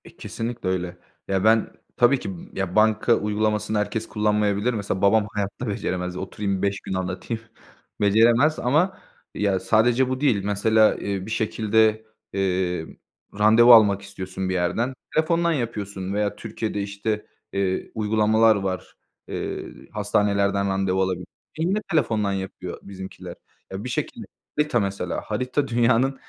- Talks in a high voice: No, low, 105 Hz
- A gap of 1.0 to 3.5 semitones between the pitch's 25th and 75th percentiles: Yes, average, 2.8 semitones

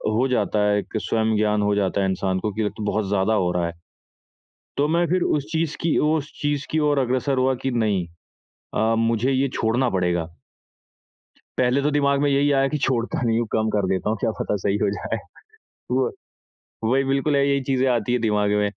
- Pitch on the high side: No, low, 120 Hz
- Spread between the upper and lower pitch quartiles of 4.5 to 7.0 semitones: Yes, average, 5.1 semitones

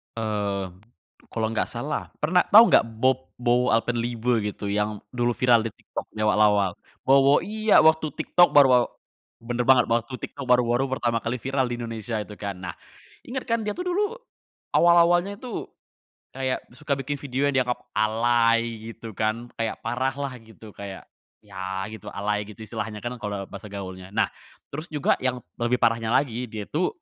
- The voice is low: Yes, low, 120 Hz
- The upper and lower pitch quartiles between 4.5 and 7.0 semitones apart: No, average, 3.8 semitones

